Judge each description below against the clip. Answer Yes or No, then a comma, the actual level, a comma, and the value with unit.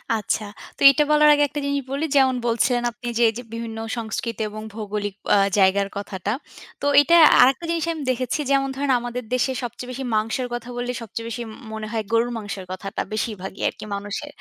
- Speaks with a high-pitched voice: Yes, high, 235 Hz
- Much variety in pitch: No, average, 3.6 semitones